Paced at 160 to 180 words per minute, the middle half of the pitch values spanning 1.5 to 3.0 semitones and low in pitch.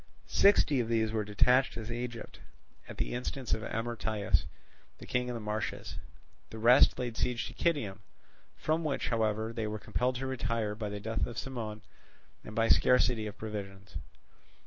Yes: average, 170 wpm; narrow, 2.5 semitones; low, 115 Hz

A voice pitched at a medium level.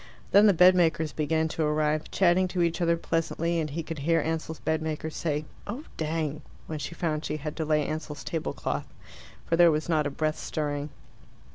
Yes: medium, 160 Hz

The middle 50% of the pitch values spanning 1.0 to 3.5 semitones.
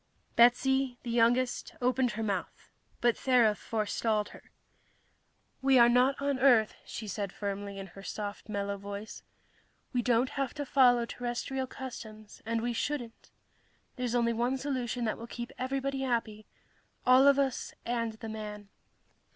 Yes: average, 3.0 semitones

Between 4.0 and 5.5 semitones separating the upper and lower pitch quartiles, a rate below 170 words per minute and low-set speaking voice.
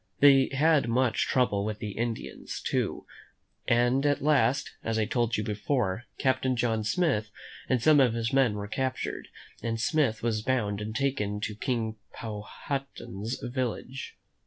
No: average, 3.6 semitones; average, 150 wpm; low, 120 Hz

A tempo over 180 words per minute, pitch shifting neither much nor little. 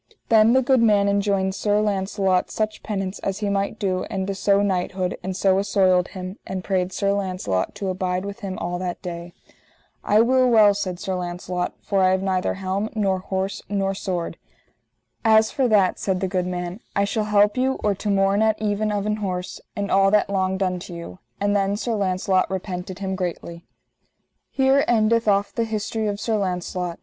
No: average, 195 wpm; narrow, 2.1 semitones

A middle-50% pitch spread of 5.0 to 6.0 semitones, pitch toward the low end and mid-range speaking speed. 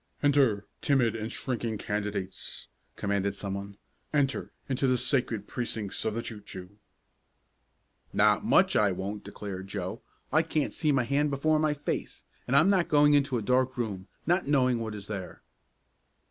Yes: wide, 5.6 semitones; low, 115 Hz; average, 160 wpm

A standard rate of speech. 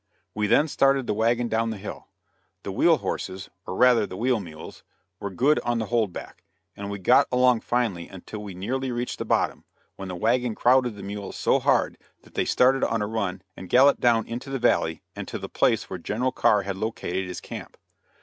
No: fast, 210 wpm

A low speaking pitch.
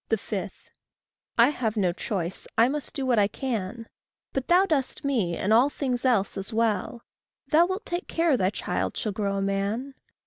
No: high, 230 Hz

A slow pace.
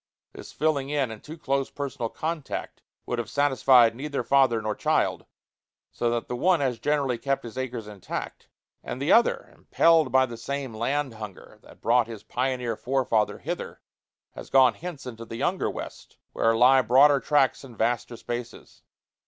No: average, 170 wpm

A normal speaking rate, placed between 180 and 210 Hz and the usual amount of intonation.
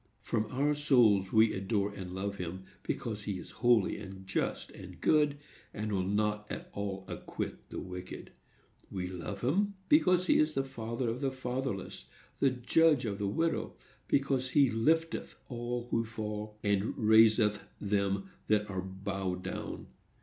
No: average, 155 wpm; low, 110 Hz; average, 4.8 semitones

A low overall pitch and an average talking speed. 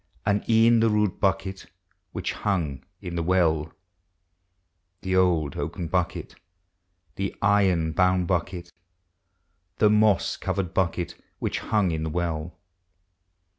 No: very low, 90 Hz; slow, 120 wpm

